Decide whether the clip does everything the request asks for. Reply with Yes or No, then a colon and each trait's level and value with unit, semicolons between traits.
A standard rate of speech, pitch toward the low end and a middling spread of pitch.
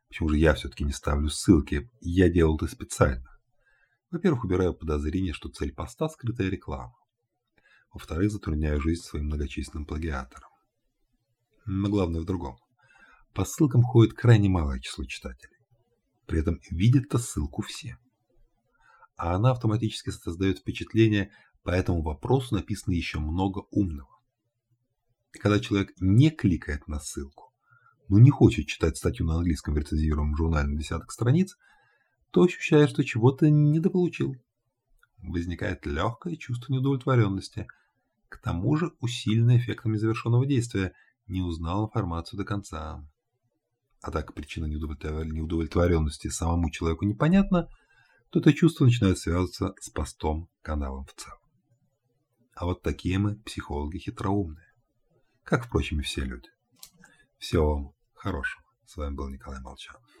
No: average, 130 wpm; low, 100 Hz; wide, 7.0 semitones